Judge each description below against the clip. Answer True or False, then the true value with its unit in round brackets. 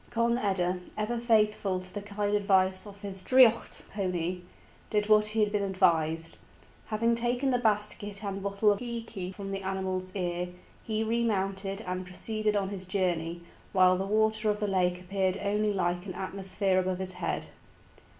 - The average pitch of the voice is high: True (195 Hz)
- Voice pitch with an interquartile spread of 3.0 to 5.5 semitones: False (2.4 semitones)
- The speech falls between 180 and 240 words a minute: False (170 wpm)